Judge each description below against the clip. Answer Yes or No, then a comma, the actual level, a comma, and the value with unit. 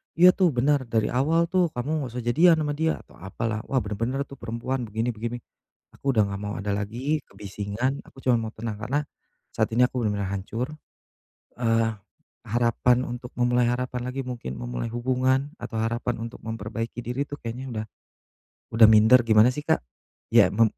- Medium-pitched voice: No, low, 120 Hz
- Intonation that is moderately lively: Yes, average, 3.0 semitones